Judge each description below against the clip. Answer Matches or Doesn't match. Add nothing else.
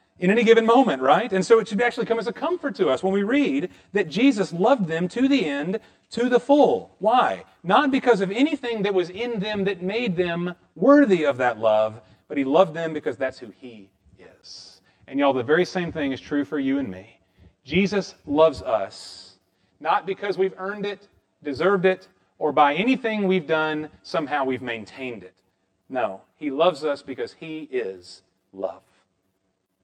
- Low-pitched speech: Doesn't match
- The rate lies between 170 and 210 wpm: Matches